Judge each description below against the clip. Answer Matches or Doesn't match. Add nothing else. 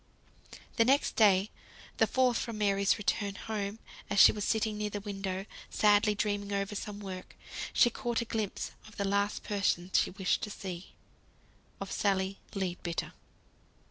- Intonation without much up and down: Matches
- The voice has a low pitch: Doesn't match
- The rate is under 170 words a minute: Matches